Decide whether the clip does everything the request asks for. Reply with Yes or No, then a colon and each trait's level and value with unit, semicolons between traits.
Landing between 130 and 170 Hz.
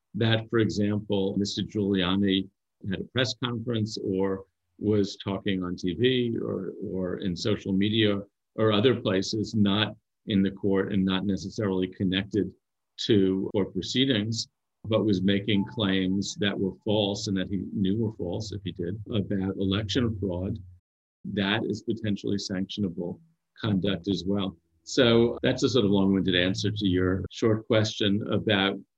No: low, 100 Hz